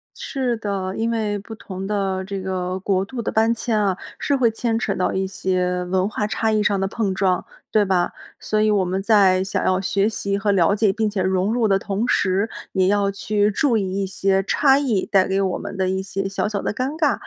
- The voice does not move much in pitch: Yes, narrow, 2.3 semitones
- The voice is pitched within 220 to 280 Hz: No, high, 200 Hz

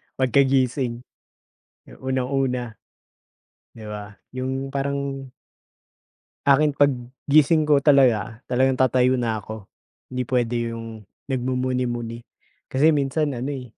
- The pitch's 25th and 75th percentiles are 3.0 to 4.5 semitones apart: No, narrow, 2.4 semitones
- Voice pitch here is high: No, low, 130 Hz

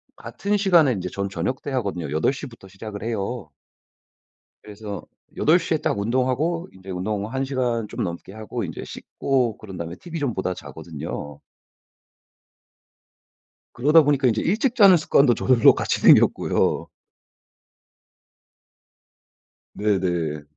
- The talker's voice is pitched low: Yes, low, 115 Hz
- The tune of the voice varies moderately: No, wide, 6.6 semitones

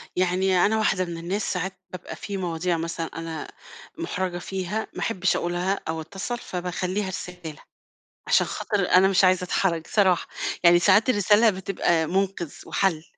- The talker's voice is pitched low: No, medium, 185 Hz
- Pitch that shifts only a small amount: Yes, narrow, 2.1 semitones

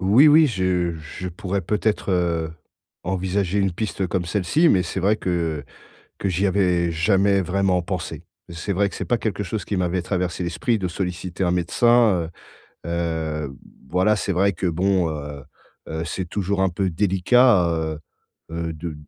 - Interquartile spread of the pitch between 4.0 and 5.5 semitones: No, average, 2.8 semitones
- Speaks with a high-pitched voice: No, very low, 90 Hz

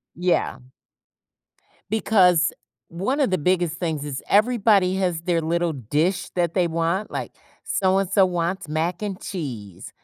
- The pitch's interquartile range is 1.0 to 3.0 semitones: Yes, average, 2.7 semitones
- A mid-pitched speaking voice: Yes, medium, 175 Hz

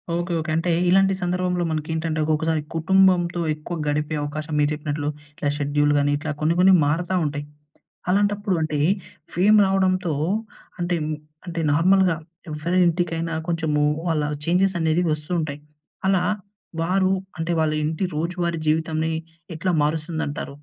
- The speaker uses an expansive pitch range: No, average, 2.8 semitones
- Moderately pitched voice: Yes, medium, 165 Hz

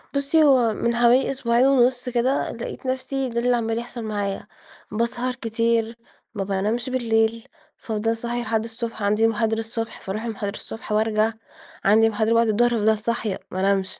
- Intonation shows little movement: Yes, narrow, 1.8 semitones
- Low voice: No, high, 230 Hz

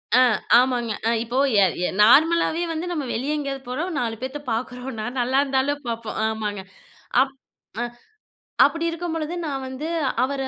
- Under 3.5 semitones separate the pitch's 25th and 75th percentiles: No, average, 3.9 semitones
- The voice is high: Yes, very high, 265 Hz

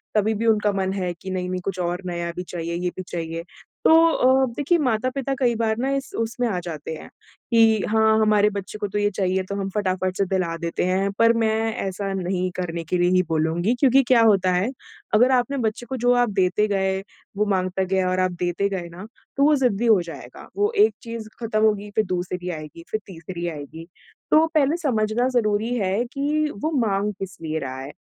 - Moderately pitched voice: No, high, 200 Hz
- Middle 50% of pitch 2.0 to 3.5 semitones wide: No, average, 4.0 semitones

